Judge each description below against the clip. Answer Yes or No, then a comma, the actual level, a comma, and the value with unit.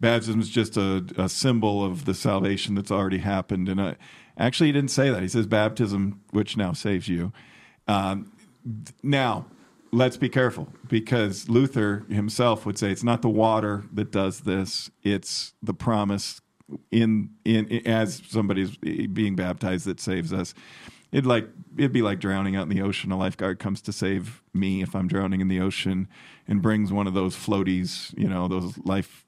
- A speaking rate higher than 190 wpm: No, average, 180 wpm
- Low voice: Yes, low, 100 Hz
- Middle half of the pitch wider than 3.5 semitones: No, average, 2.9 semitones